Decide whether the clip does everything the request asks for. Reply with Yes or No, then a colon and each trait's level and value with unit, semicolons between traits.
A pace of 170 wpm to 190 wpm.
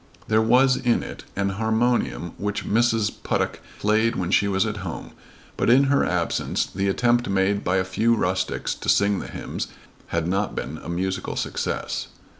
Yes: average, 175 wpm